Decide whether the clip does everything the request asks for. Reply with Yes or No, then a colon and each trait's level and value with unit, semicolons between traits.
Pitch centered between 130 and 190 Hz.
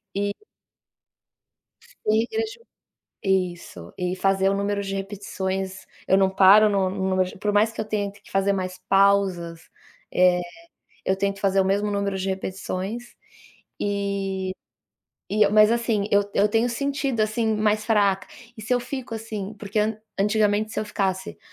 No: high, 200 Hz